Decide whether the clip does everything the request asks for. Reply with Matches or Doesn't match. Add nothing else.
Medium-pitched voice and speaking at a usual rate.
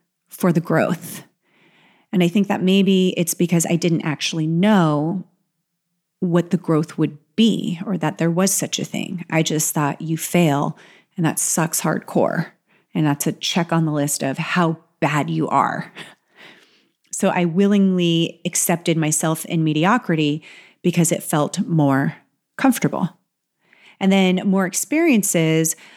Matches